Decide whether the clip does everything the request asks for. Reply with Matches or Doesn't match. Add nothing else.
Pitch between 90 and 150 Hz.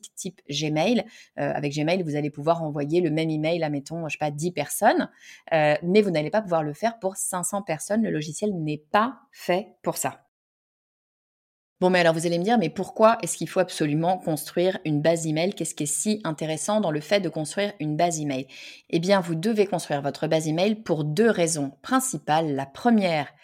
Doesn't match